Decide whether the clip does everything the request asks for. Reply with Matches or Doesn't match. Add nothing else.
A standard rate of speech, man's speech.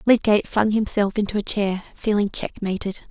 Doesn't match